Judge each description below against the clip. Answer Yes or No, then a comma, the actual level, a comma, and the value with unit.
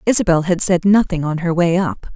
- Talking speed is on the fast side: Yes, fast, 225 wpm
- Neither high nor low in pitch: Yes, medium, 175 Hz